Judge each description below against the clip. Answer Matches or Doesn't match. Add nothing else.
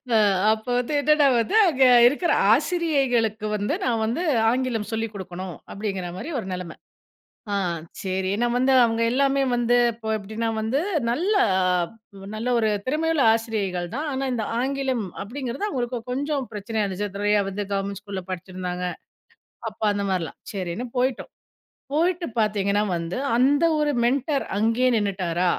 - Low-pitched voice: Doesn't match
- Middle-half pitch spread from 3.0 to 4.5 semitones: Doesn't match